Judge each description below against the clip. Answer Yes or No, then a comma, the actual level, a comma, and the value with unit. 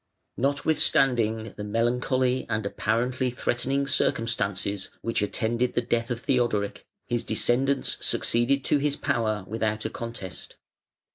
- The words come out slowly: Yes, slow, 120 wpm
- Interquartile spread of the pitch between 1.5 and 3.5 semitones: Yes, average, 2.8 semitones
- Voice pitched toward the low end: Yes, low, 120 Hz